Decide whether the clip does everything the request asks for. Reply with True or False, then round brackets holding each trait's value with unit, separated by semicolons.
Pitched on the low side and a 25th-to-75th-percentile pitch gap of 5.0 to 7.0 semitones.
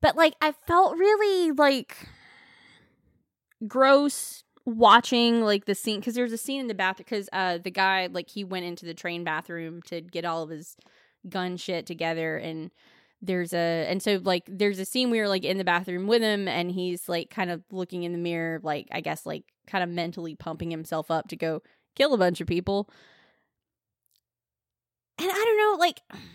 False (185 Hz; 5.3 semitones)